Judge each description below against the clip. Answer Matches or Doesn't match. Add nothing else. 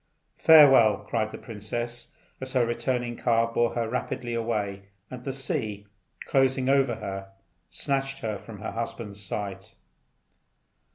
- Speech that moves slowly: Matches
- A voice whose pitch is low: Matches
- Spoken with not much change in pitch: Doesn't match